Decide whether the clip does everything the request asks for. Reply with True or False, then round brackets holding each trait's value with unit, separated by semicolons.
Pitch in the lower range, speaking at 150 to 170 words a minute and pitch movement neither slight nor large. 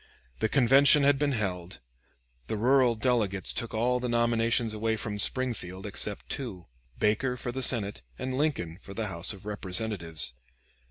True (110 Hz; 155 wpm; 4.0 semitones)